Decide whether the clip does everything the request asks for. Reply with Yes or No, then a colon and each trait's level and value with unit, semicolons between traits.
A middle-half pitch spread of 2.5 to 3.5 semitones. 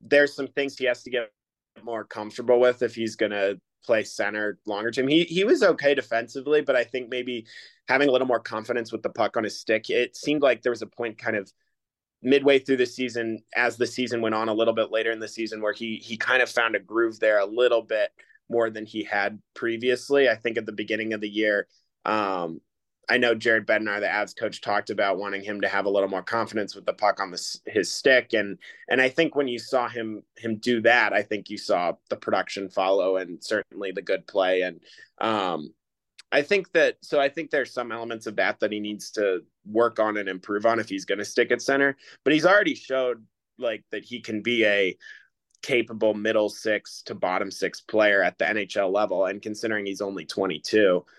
Yes: average, 2.9 semitones